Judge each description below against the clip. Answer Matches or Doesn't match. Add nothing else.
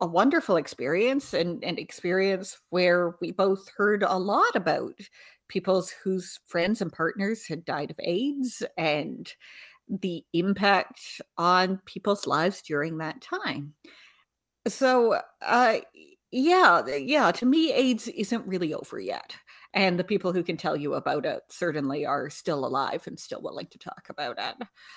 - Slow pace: Doesn't match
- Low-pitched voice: Doesn't match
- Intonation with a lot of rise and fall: Matches